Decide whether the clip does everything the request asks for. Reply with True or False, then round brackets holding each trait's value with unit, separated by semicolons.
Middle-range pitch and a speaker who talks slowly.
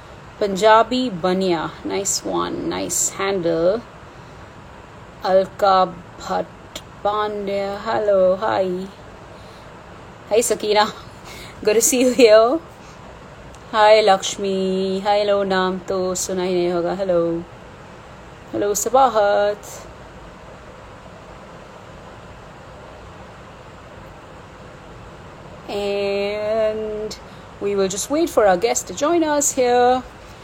False (200 Hz; 85 wpm)